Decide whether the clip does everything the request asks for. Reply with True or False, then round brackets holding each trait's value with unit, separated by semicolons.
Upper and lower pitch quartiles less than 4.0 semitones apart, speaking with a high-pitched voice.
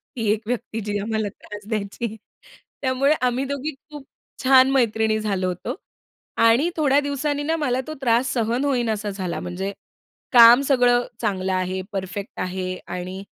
False (4.7 semitones; 230 Hz)